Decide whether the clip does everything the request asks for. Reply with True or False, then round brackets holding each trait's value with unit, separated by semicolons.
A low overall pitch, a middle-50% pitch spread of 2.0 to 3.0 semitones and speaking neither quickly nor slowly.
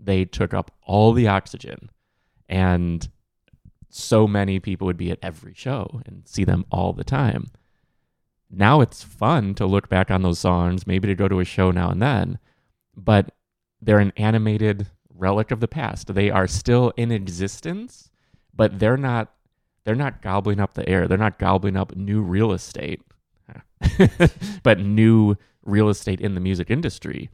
True (100 Hz; 2.7 semitones; 165 wpm)